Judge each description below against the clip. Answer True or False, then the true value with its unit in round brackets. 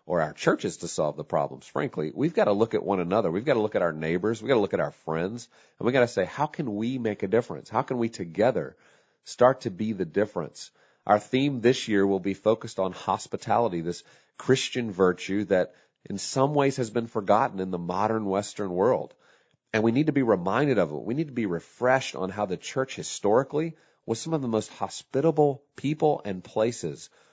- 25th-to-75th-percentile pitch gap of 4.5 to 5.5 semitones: True (4.9 semitones)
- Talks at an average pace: False (220 wpm)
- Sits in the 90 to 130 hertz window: True (110 Hz)